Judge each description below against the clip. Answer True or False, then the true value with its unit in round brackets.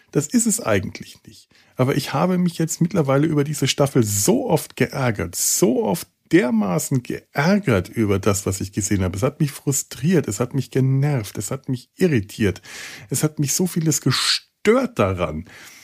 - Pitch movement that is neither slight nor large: False (6.0 semitones)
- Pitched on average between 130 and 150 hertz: True (135 Hz)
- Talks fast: False (175 wpm)